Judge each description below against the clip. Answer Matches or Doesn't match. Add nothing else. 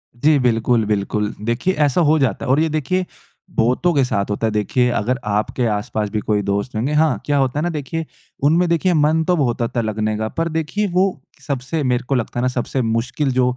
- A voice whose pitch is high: Doesn't match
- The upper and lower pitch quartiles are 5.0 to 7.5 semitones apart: Matches